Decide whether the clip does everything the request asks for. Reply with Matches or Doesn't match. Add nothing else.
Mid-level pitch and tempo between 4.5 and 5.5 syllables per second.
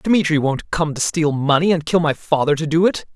Matches